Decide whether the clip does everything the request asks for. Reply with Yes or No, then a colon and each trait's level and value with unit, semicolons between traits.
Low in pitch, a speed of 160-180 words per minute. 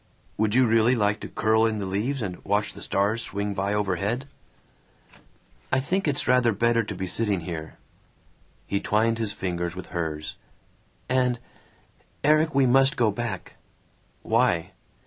No: low, 110 Hz; average, 150 wpm